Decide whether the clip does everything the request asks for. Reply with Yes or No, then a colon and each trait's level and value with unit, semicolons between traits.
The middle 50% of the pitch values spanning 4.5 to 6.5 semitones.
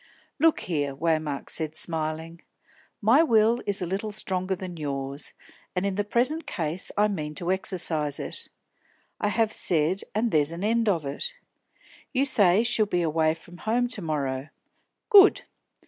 Yes: wide, 5.5 semitones